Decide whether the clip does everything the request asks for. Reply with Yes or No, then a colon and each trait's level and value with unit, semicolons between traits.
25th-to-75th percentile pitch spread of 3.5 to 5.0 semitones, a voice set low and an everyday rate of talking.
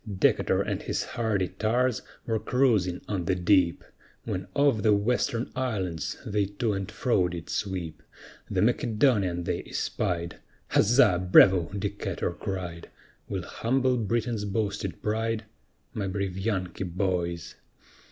No: average, 3.9 semitones; low, 100 Hz; slow, 125 wpm